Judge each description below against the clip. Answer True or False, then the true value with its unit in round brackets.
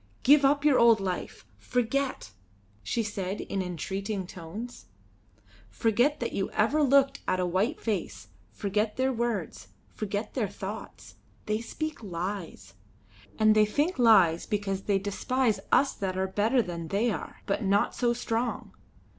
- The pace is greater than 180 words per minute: False (145 wpm)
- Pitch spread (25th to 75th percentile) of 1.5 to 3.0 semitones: False (4.1 semitones)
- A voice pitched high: True (215 Hz)